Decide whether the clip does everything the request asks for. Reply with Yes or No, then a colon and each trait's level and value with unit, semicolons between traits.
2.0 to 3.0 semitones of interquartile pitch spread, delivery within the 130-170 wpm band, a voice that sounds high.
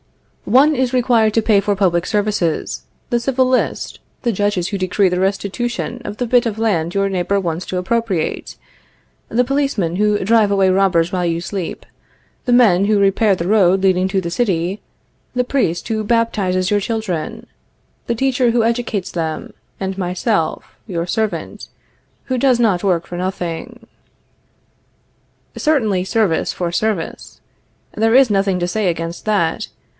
No: average, 4.2 semitones; average, 155 wpm; high, 200 Hz